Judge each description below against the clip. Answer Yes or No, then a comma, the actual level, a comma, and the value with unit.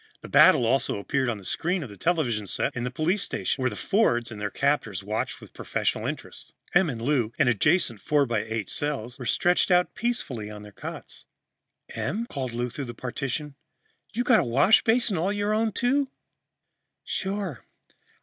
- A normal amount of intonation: No, wide, 8.2 semitones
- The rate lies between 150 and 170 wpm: No, average, 185 wpm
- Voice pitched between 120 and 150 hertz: Yes, medium, 140 Hz